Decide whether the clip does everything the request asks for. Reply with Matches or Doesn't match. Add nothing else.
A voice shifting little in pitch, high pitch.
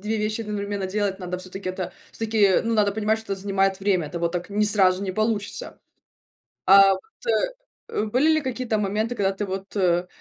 Matches